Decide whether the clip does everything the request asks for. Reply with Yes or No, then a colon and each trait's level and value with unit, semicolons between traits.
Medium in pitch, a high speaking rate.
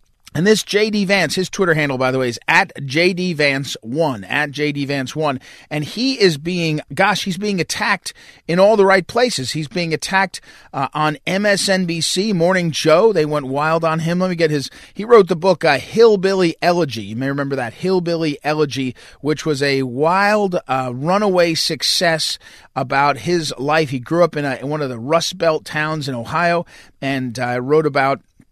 No: medium, 160 Hz; average, 185 wpm